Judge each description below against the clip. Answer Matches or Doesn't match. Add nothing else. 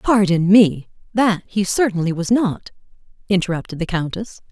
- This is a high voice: Matches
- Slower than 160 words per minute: Matches